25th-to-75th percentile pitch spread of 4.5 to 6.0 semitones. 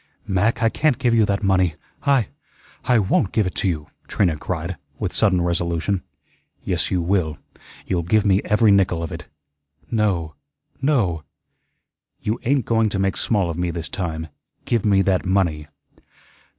No: average, 3.8 semitones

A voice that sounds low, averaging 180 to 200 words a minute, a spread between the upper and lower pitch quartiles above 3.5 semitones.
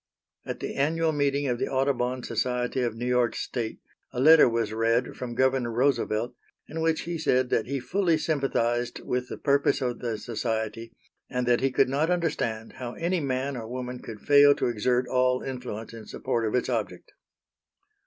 No: low, 125 Hz; average, 185 wpm; average, 2.9 semitones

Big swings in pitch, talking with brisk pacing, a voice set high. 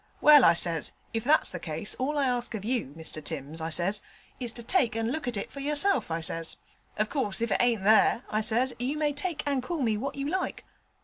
Yes: wide, 6.0 semitones; fast, 240 wpm; high, 235 Hz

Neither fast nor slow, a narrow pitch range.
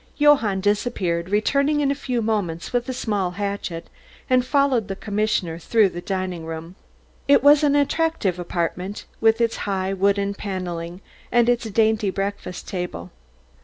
No: average, 150 wpm; average, 4.8 semitones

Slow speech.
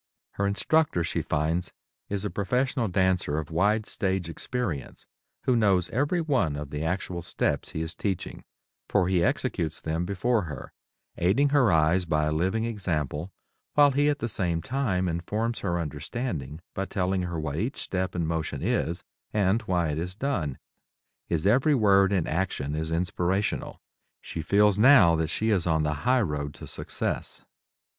No: average, 165 wpm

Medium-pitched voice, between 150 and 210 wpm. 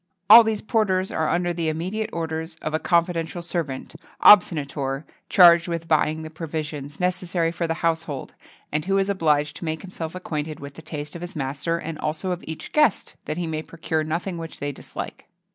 Yes: medium, 165 Hz; average, 195 wpm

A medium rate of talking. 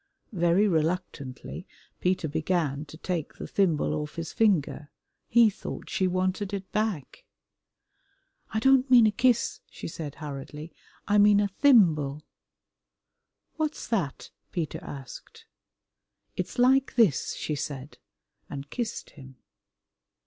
No: slow, 120 wpm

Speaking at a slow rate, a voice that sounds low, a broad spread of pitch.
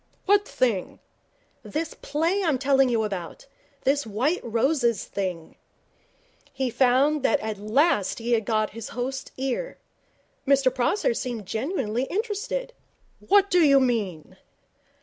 No: slow, 130 wpm; very high, 260 Hz; wide, 6.0 semitones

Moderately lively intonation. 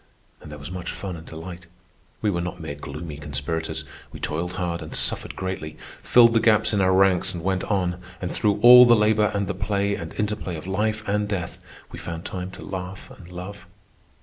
Yes: average, 3.3 semitones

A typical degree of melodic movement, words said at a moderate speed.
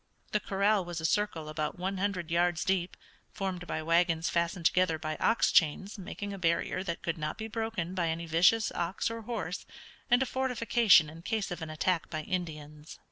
Yes: average, 3.8 semitones; average, 190 wpm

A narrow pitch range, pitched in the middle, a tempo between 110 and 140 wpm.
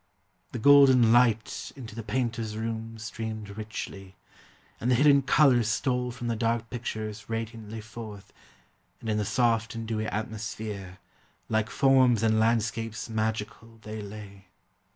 No: narrow, 1.6 semitones; low, 115 Hz; slow, 135 wpm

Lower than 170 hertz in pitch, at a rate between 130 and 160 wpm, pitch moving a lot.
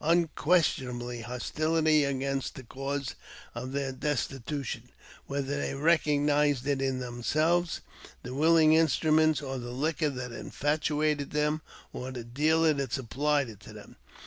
No: medium, 140 Hz; slow, 135 wpm; average, 3.0 semitones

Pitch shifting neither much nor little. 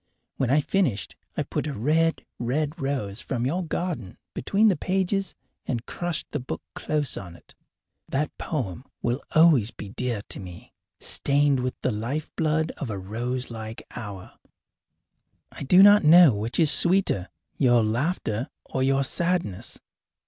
No: wide, 6.1 semitones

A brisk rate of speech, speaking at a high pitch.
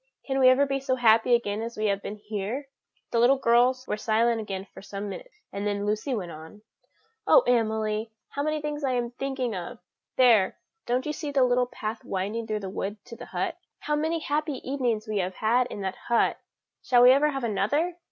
Yes: fast, 210 wpm; high, 235 Hz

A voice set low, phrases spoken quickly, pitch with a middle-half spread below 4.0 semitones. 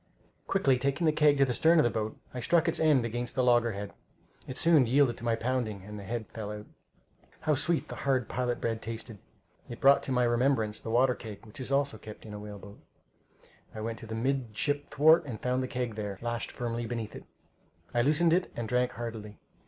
Yes: low, 120 Hz; fast, 220 wpm; average, 3.6 semitones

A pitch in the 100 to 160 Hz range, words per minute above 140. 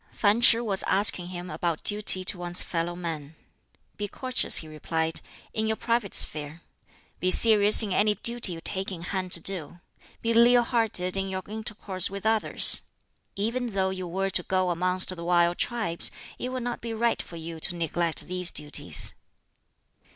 No: high, 190 Hz; average, 175 wpm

